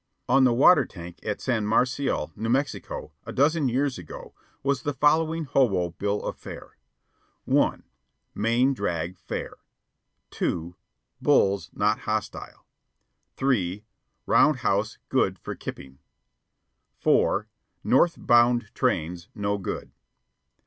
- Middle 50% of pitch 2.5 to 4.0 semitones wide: No, wide, 5.5 semitones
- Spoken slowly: Yes, slow, 115 wpm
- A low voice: Yes, low, 115 Hz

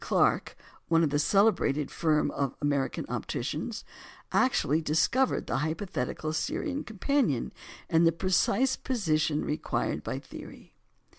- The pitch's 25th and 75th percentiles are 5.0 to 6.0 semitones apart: Yes, wide, 5.5 semitones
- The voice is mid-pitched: Yes, medium, 160 Hz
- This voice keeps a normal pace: No, slow, 120 wpm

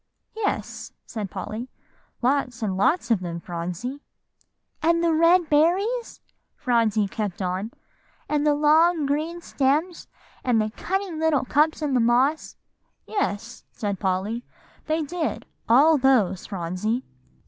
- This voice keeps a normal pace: No, slow, 125 wpm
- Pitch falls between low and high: No, very high, 265 Hz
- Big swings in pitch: Yes, wide, 6.9 semitones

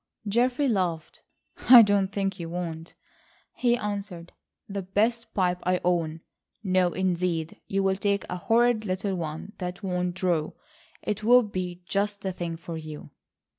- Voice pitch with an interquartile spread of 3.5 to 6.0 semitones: No, average, 2.9 semitones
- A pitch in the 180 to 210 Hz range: Yes, medium, 185 Hz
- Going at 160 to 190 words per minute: No, average, 140 wpm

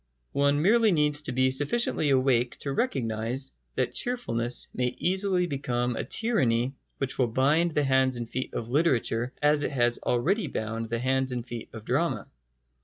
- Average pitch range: Yes, average, 3.7 semitones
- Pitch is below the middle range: Yes, low, 130 Hz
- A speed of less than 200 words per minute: Yes, average, 170 wpm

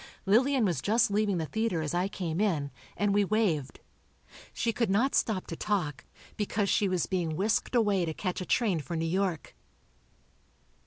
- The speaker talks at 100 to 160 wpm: No, average, 175 wpm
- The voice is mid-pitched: No, high, 195 Hz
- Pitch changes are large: No, average, 4.1 semitones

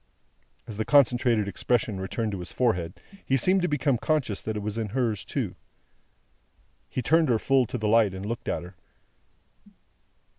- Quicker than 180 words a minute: No, average, 175 wpm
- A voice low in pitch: Yes, low, 115 Hz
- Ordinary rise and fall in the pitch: Yes, average, 3.9 semitones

